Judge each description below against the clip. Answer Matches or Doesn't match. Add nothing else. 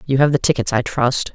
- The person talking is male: Doesn't match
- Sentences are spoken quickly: Matches